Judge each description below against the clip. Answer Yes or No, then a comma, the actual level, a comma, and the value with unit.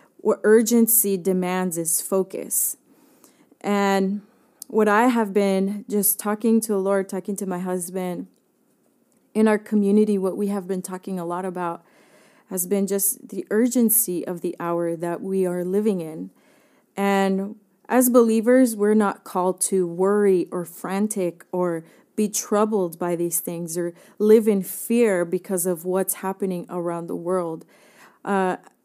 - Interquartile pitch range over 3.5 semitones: No, average, 2.8 semitones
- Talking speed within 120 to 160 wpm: Yes, average, 150 wpm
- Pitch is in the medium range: No, high, 195 Hz